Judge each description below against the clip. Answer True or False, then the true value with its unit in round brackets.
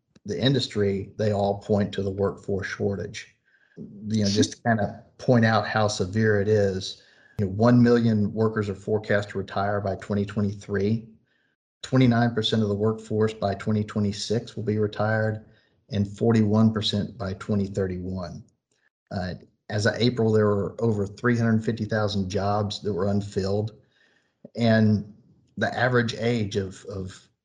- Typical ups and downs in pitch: False (1.7 semitones)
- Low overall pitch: True (105 Hz)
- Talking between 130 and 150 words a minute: True (140 wpm)